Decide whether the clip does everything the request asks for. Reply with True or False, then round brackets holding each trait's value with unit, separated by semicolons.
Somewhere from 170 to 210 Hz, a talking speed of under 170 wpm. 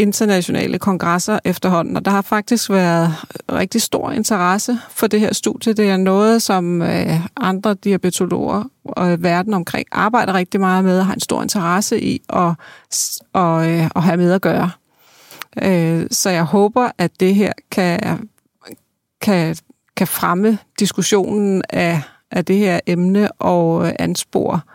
True (190 Hz; 145 wpm)